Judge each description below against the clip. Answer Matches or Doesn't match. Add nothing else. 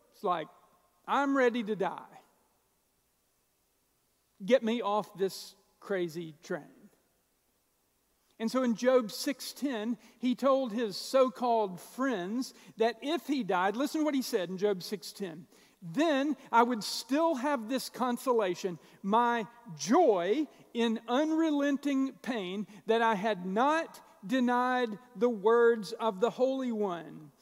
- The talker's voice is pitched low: Doesn't match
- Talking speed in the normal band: Doesn't match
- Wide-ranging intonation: Doesn't match